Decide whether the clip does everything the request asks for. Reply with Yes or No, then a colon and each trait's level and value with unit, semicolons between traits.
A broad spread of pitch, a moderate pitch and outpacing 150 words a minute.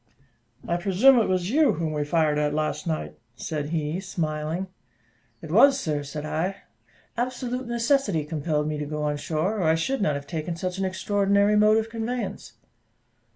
Yes: wide, 5.7 semitones; medium, 170 Hz; average, 175 wpm